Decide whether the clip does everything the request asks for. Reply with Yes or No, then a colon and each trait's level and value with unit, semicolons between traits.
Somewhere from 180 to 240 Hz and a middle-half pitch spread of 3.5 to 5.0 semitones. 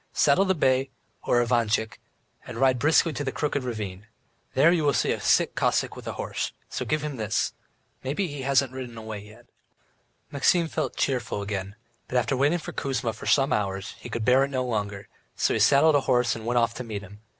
No: low, 125 Hz; average, 4.2 semitones